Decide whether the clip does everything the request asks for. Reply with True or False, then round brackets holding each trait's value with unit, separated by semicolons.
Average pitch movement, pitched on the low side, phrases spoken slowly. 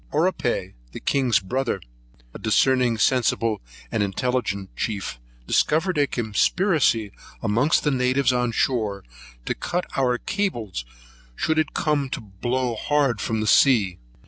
True (4.5 semitones; 125 Hz; 130 wpm)